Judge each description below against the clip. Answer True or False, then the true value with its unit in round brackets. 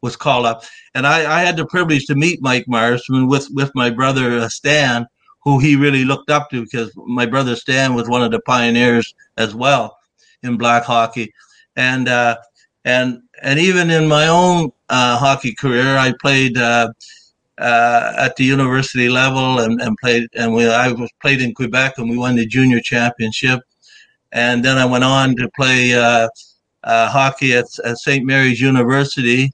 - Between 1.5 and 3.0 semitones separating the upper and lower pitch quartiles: True (2.4 semitones)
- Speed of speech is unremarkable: True (175 wpm)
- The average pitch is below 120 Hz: False (125 Hz)